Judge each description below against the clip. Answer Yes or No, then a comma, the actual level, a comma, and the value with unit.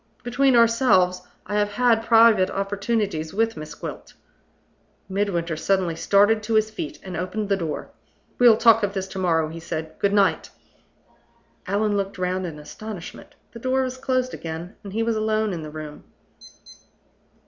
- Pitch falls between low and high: No, high, 200 Hz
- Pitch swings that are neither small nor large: Yes, average, 4.0 semitones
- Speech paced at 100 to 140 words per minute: No, average, 165 wpm